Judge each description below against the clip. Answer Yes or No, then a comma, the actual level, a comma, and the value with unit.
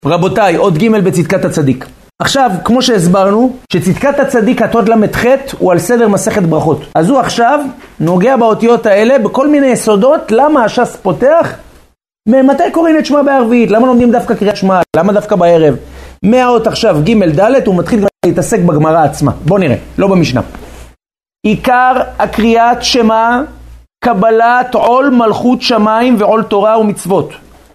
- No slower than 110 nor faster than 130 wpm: No, average, 145 wpm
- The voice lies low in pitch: No, high, 225 Hz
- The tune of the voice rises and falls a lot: No, average, 4.7 semitones